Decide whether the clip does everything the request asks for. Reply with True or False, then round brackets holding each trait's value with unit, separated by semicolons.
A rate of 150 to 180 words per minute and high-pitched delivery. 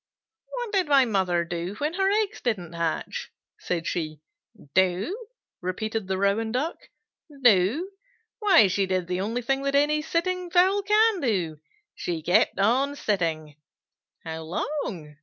False (140 wpm; 220 Hz)